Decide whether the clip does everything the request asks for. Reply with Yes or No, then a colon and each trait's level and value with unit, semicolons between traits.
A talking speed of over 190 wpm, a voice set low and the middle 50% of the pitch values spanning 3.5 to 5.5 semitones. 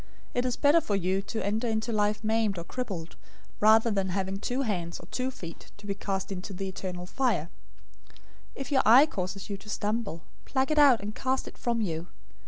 No: fast, 205 wpm; high, 210 Hz; average, 4.1 semitones